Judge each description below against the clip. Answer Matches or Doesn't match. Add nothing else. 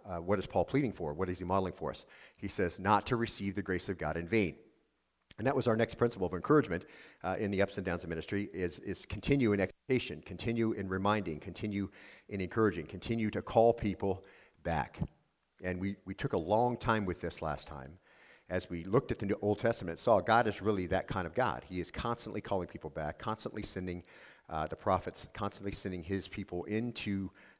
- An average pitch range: Matches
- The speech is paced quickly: Matches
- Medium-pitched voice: Doesn't match